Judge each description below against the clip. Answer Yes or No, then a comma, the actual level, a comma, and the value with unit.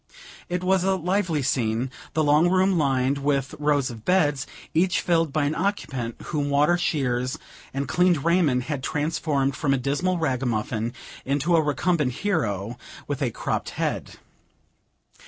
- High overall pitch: No, medium, 145 Hz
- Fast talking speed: No, average, 150 wpm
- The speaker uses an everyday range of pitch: Yes, average, 4.7 semitones